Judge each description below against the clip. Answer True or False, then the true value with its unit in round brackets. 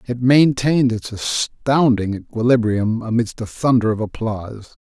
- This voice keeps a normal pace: False (125 wpm)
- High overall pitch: False (115 Hz)